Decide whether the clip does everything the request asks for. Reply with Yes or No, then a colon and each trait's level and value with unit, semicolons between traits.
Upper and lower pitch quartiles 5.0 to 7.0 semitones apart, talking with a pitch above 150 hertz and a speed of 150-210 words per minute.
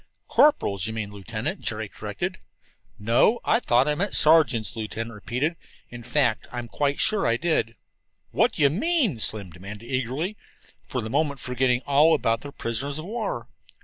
No: wide, 5.4 semitones; low, 125 Hz; average, 170 wpm